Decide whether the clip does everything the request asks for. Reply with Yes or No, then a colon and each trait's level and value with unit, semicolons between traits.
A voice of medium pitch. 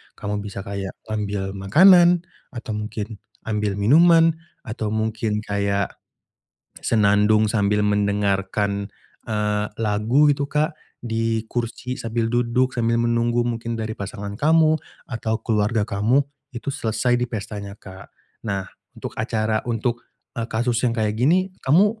No: low, 110 Hz